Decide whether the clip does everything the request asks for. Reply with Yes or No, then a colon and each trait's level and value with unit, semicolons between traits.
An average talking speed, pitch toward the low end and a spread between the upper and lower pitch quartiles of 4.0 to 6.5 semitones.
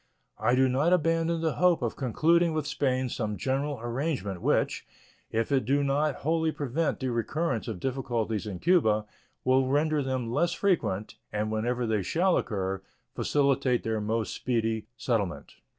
Yes: average, 155 wpm; low, 130 Hz; average, 5.3 semitones